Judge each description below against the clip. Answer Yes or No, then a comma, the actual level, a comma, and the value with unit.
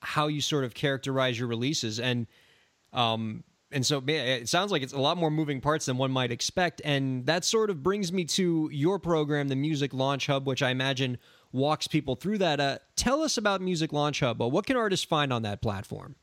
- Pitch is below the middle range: No, medium, 145 Hz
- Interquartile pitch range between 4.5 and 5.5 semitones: No, average, 3.8 semitones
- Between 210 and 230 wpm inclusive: Yes, fast, 220 wpm